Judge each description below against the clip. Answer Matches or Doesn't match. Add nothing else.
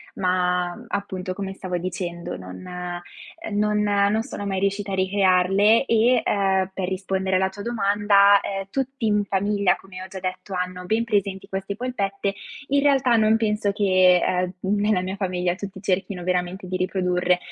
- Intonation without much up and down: Matches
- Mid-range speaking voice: Doesn't match